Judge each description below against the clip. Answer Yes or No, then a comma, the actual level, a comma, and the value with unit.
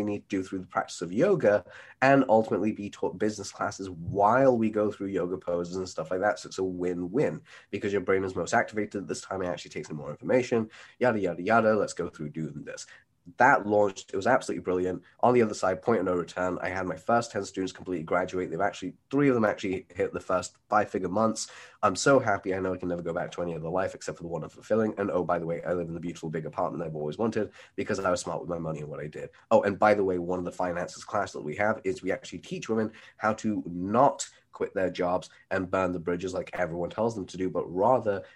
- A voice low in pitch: Yes, very low, 95 Hz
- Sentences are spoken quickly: Yes, fast, 260 wpm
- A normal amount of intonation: Yes, average, 3.1 semitones